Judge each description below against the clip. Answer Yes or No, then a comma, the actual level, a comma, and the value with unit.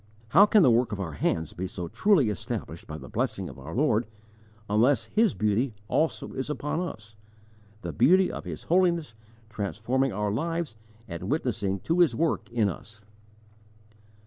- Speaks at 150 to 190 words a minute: Yes, average, 165 wpm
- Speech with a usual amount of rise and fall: No, wide, 8.0 semitones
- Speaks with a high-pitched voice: No, low, 115 Hz